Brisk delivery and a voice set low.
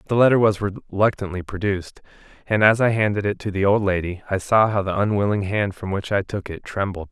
Yes: fast, 220 wpm; low, 100 Hz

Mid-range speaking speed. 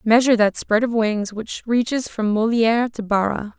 Yes: average, 185 wpm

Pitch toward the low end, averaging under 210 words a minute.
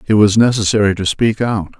Yes: low, 105 Hz; average, 200 wpm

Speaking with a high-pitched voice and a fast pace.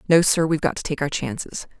No: medium, 155 Hz; fast, 235 wpm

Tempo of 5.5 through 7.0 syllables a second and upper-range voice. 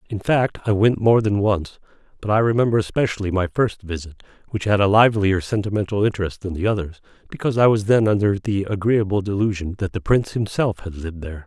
No: 6.3 syllables/s; low, 100 Hz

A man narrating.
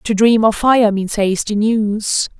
No: female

